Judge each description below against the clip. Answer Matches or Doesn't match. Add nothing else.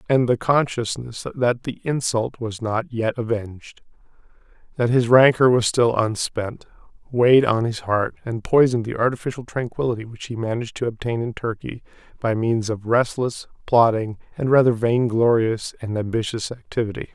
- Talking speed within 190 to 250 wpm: Doesn't match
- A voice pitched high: Doesn't match